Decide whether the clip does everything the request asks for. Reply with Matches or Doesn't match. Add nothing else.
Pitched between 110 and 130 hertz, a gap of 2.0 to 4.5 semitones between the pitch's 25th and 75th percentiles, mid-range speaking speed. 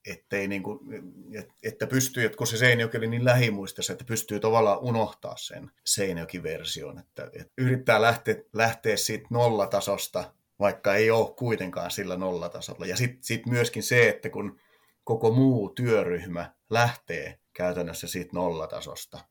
Matches